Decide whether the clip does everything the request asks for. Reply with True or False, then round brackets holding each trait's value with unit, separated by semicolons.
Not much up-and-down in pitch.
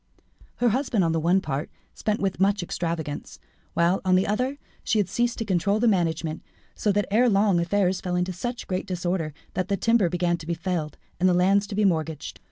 False (3.2 semitones)